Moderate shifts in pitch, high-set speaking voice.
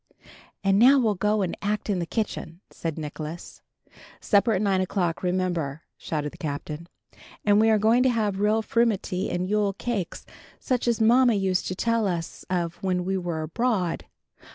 Yes: average, 4.1 semitones; high, 195 Hz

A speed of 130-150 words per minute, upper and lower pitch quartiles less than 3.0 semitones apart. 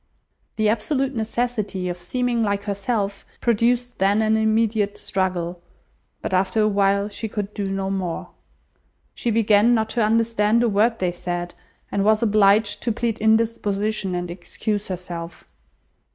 Yes: average, 145 wpm; narrow, 2.6 semitones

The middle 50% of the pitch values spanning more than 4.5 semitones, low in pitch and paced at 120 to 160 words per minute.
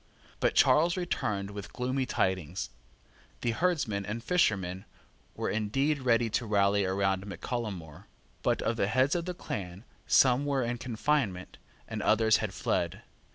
Yes: average, 5.1 semitones; low, 110 Hz; average, 155 wpm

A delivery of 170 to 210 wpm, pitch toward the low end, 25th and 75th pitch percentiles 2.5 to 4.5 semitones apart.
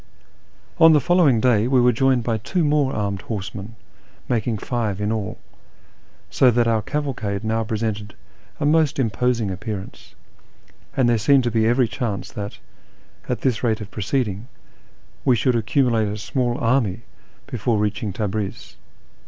No: average, 155 wpm; low, 115 Hz; average, 3.3 semitones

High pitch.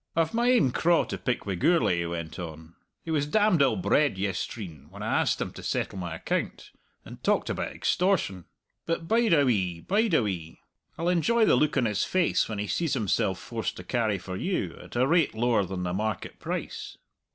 No: low, 120 Hz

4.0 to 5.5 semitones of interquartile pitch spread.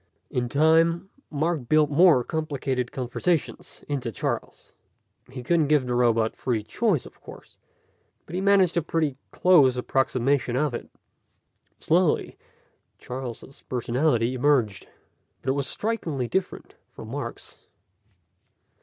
Yes: average, 4.7 semitones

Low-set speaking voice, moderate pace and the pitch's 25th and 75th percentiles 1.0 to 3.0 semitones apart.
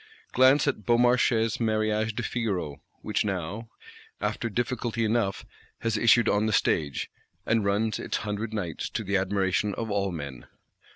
Yes: low, 110 Hz; average, 160 wpm; narrow, 2.6 semitones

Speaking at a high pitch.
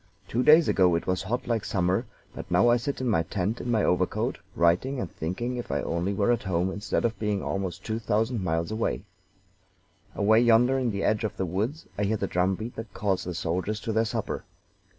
No: low, 105 Hz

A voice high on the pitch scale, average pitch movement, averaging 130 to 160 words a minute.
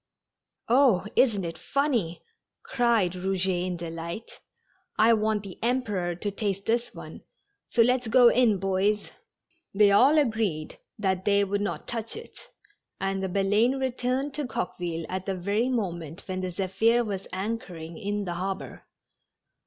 Yes: high, 200 Hz; average, 4.1 semitones; average, 145 wpm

